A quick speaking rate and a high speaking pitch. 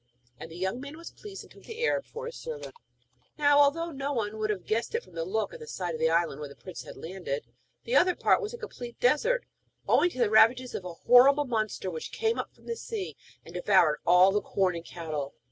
Yes: fast, 245 wpm; high, 230 Hz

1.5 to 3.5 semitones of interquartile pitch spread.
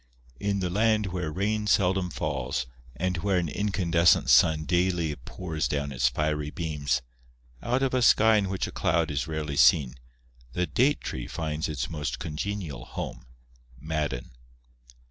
No: average, 4.6 semitones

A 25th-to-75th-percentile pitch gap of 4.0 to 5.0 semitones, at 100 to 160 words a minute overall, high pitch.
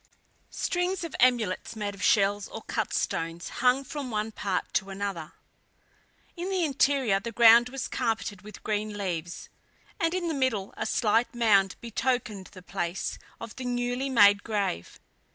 Yes: average, 4.3 semitones; average, 155 wpm; high, 220 Hz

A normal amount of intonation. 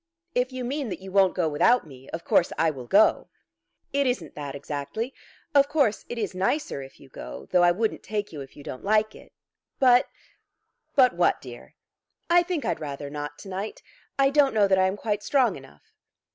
No: wide, 8.9 semitones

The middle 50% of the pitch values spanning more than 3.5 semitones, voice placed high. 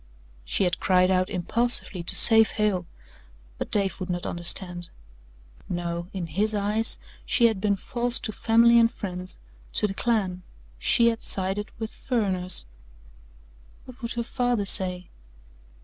Yes: average, 3.9 semitones; high, 200 Hz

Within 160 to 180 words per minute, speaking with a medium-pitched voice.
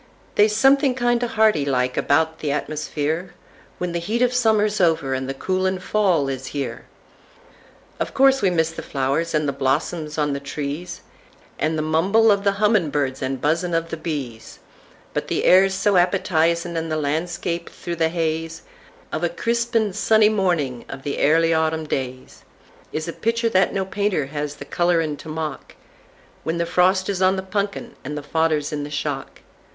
Yes: average, 165 wpm; medium, 165 Hz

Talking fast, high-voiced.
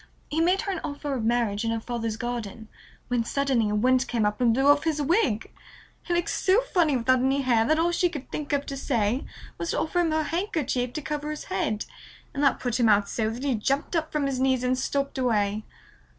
Yes: fast, 235 wpm; very high, 265 Hz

